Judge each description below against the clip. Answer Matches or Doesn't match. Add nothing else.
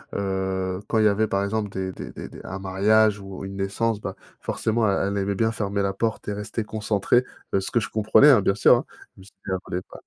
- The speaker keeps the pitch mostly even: Matches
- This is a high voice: Doesn't match